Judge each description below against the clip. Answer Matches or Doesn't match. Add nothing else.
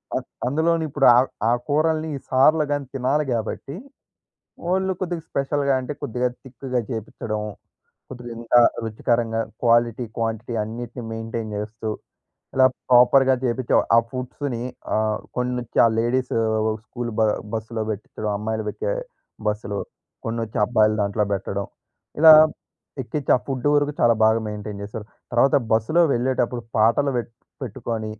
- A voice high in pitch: Doesn't match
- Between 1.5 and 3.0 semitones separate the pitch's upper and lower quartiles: Doesn't match